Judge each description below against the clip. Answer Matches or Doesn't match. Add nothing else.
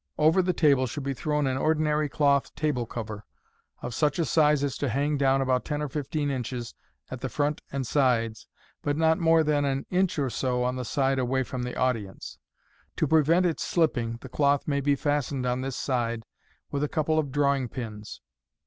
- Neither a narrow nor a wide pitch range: Matches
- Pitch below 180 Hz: Matches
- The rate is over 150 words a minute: Matches